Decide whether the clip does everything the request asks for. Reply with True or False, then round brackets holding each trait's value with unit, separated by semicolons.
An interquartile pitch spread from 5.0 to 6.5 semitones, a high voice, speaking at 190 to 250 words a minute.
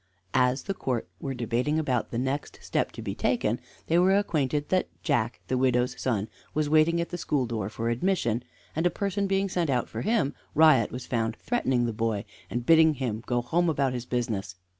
False (5.4 semitones; 130 Hz; 205 wpm)